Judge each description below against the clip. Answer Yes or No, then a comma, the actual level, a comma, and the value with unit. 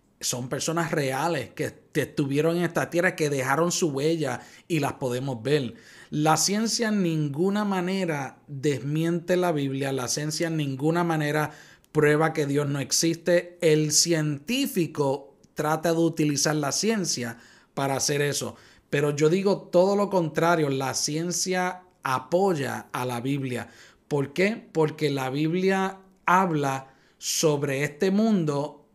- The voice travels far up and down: No, average, 3.9 semitones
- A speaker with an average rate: Yes, average, 135 wpm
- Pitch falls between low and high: Yes, medium, 155 Hz